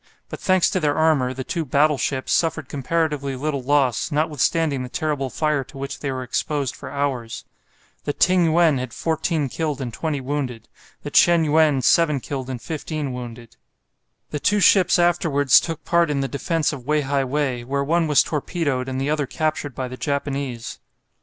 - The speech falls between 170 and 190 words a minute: Yes, average, 180 wpm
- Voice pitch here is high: No, medium, 145 Hz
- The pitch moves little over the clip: No, average, 3.2 semitones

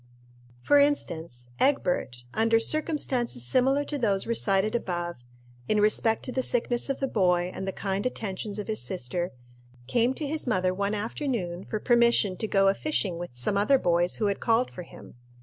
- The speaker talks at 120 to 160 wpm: No, average, 180 wpm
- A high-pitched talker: Yes, high, 210 Hz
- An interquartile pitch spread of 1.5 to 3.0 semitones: No, average, 5.1 semitones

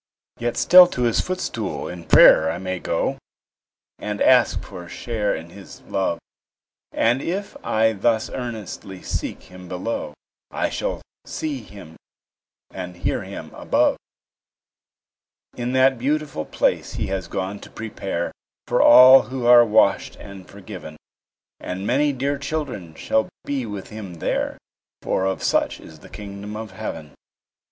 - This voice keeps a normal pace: Yes, average, 145 wpm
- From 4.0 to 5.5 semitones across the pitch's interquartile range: Yes, average, 5.1 semitones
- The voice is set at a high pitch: No, low, 105 Hz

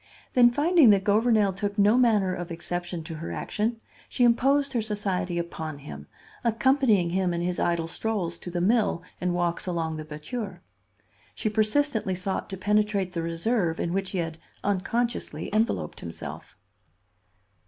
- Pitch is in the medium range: No, high, 195 Hz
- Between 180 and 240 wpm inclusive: No, average, 155 wpm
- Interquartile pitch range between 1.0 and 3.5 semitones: No, average, 4.5 semitones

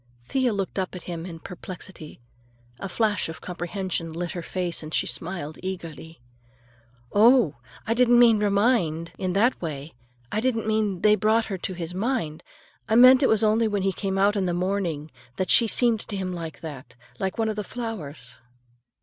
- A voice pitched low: No, high, 190 Hz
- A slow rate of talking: No, average, 185 wpm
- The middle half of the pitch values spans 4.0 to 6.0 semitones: Yes, average, 4.6 semitones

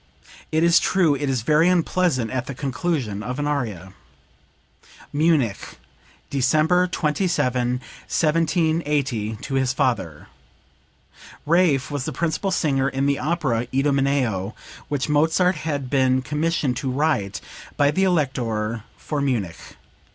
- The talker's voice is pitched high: No, medium, 140 Hz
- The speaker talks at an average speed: No, slow, 120 wpm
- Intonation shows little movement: No, average, 4.1 semitones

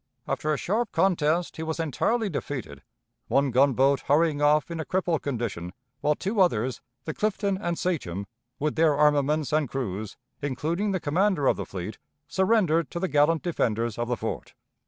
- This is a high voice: No, medium, 150 Hz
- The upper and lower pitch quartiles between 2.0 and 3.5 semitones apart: No, average, 4.5 semitones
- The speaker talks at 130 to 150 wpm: No, average, 170 wpm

